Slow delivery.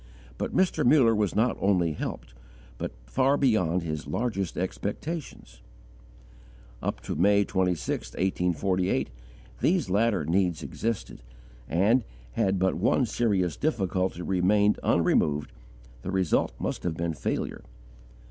Yes: slow, 120 wpm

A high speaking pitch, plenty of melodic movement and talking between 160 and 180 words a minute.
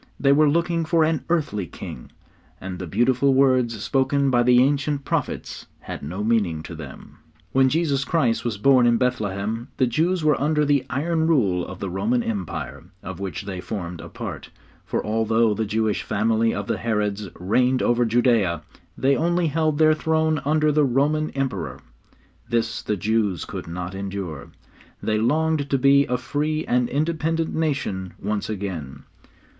No: low, 120 Hz; wide, 6.3 semitones; average, 165 wpm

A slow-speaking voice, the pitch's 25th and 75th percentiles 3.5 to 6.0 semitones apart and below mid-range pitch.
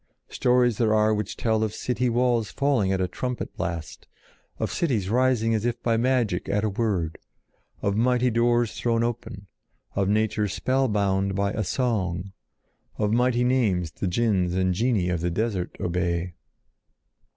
No: average, 155 wpm; average, 4.0 semitones; low, 110 Hz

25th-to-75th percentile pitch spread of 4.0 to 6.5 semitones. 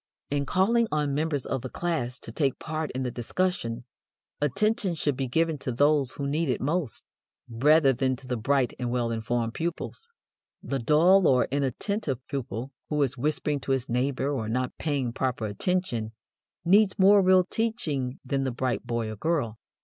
Yes: average, 4.7 semitones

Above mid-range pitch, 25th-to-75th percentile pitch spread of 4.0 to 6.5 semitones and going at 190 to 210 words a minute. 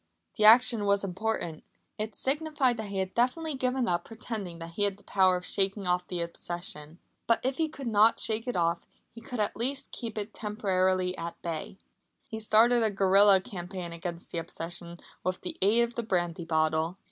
Yes: high, 200 Hz; average, 4.6 semitones; average, 195 wpm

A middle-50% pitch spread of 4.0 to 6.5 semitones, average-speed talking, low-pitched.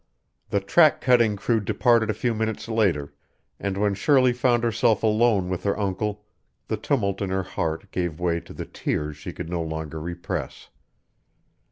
Yes: average, 4.6 semitones; average, 170 wpm; low, 100 Hz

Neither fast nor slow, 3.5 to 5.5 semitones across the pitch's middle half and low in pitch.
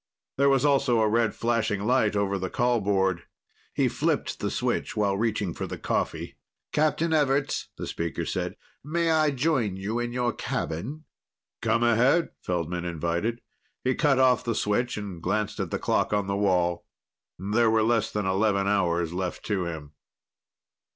Yes: average, 165 wpm; average, 4.5 semitones; low, 110 Hz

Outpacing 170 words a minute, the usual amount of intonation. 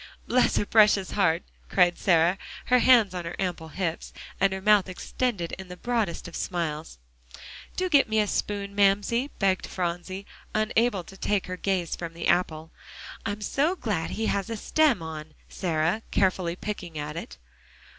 No: average, 165 wpm; average, 3.8 semitones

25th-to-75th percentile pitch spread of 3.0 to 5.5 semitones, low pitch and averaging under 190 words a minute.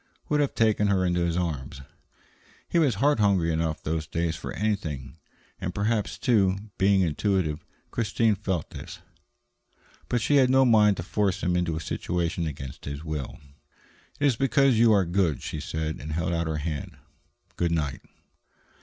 Yes: average, 5.0 semitones; very low, 90 Hz; average, 170 wpm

